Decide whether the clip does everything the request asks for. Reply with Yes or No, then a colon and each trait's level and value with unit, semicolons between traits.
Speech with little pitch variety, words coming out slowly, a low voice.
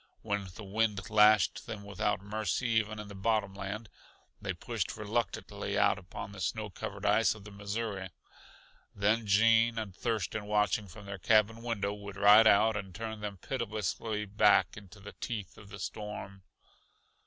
No: narrow, 1.6 semitones; average, 165 wpm; low, 105 Hz